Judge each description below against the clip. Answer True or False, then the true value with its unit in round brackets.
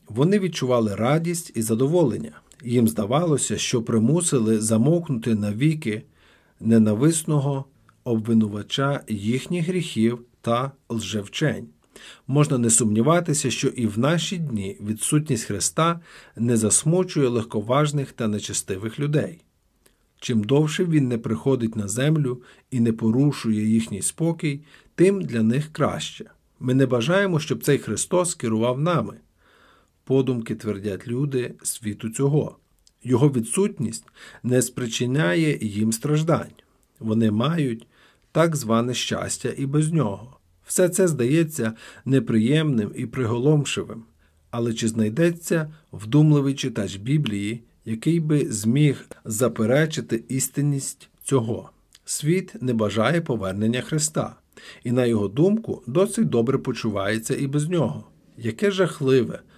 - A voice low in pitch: True (125 Hz)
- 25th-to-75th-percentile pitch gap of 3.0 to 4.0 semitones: False (5.2 semitones)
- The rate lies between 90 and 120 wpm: True (115 wpm)